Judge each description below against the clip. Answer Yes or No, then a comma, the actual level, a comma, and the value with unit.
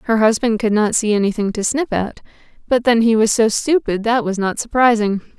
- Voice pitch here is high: Yes, high, 220 Hz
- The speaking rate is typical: No, fast, 210 wpm